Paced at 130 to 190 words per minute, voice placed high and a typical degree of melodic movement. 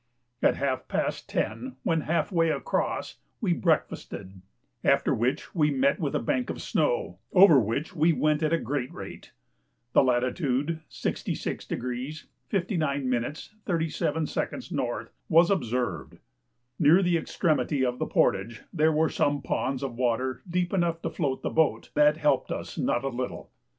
No: average, 150 wpm; medium, 150 Hz; average, 4.5 semitones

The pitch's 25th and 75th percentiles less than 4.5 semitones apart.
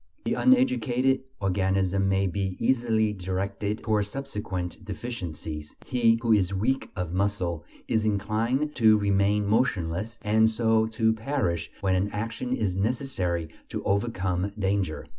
Yes: average, 3.3 semitones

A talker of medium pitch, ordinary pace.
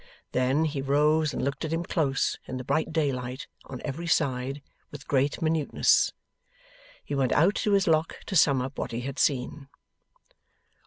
Yes: medium, 145 Hz; average, 170 wpm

